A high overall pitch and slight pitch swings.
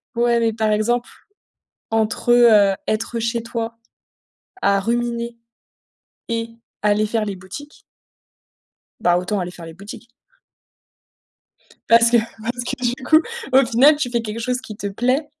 Yes: high, 230 Hz; narrow, 2.1 semitones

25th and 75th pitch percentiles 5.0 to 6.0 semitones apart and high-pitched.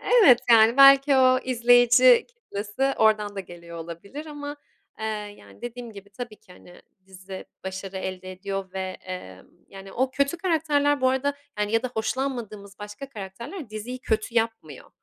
Yes: average, 5.3 semitones; high, 225 Hz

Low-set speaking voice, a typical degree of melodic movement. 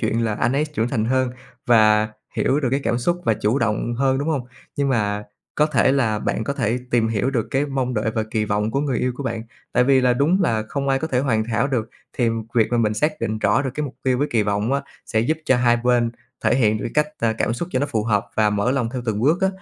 Yes: low, 120 Hz; average, 3.8 semitones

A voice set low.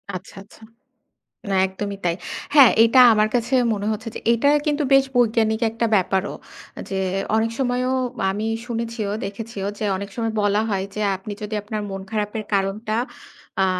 No: high, 215 Hz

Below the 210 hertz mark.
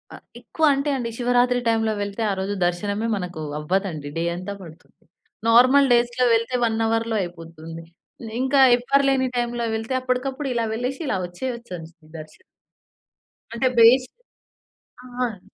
No: high, 230 Hz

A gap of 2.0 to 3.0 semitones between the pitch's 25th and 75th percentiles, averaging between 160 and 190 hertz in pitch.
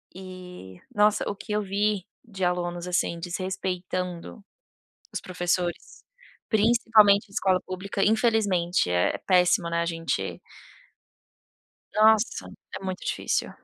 Yes: average, 2.7 semitones; medium, 185 Hz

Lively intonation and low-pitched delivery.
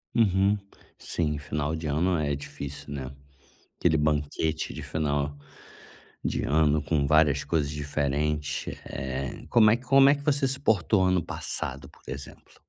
No: average, 4.4 semitones; very low, 75 Hz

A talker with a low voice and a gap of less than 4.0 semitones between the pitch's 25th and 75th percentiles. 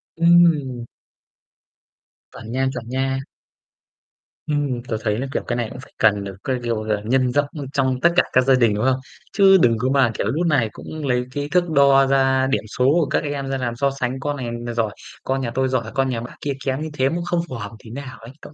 Yes: low, 130 Hz; average, 3.0 semitones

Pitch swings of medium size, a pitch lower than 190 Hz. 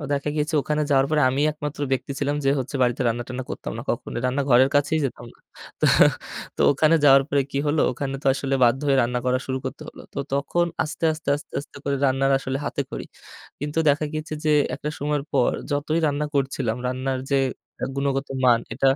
No: narrow, 2.0 semitones; medium, 140 Hz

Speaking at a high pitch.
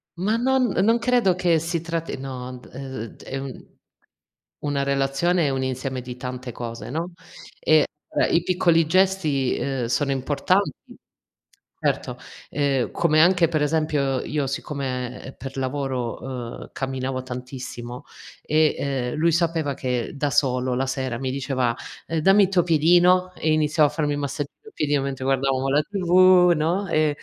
No: medium, 145 Hz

